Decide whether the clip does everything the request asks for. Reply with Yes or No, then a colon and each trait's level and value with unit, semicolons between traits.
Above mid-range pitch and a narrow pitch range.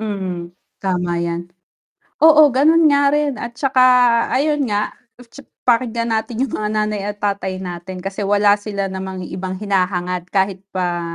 No: high, 200 Hz; average, 4.3 semitones